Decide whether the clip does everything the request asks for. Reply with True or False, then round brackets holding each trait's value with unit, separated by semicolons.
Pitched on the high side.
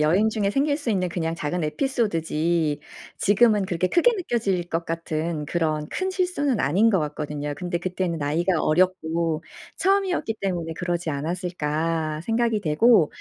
False (175 Hz)